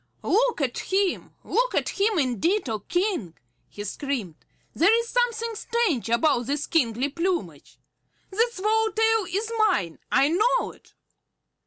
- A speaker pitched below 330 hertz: No, very high, 370 Hz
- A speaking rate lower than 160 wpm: Yes, average, 140 wpm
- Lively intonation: Yes, wide, 8.6 semitones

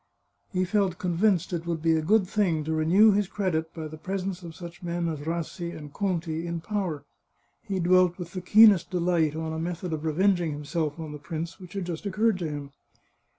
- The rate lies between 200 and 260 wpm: Yes, fast, 205 wpm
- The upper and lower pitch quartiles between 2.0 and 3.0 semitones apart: Yes, average, 2.7 semitones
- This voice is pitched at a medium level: Yes, medium, 170 Hz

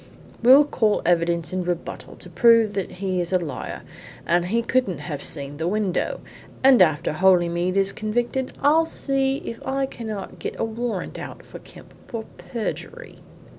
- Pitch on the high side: Yes, high, 200 Hz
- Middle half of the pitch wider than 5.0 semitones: Yes, wide, 5.6 semitones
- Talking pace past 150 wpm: Yes, average, 165 wpm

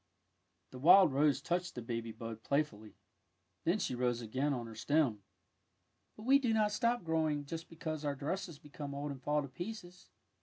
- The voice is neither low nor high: Yes, medium, 150 Hz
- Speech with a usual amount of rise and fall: No, wide, 5.7 semitones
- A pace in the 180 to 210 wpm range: Yes, average, 195 wpm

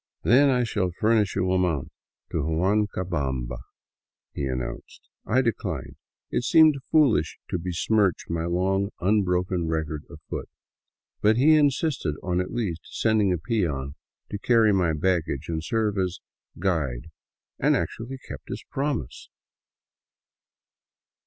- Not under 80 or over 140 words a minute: Yes, slow, 135 wpm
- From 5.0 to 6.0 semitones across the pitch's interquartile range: Yes, wide, 5.4 semitones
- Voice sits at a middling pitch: No, very low, 95 Hz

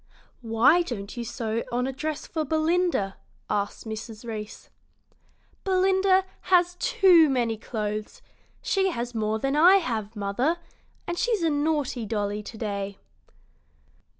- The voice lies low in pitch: No, very high, 250 Hz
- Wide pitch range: Yes, wide, 8.0 semitones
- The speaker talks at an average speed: No, slow, 130 wpm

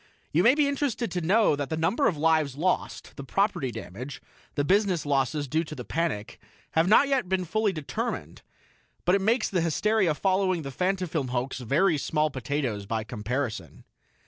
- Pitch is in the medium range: Yes, medium, 160 Hz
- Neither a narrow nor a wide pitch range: No, wide, 5.9 semitones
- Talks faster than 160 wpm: Yes, average, 175 wpm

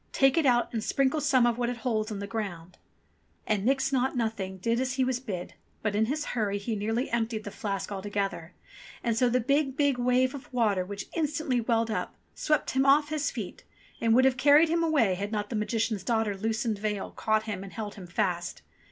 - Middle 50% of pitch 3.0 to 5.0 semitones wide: Yes, average, 4.1 semitones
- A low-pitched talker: No, high, 230 Hz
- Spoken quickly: Yes, fast, 215 wpm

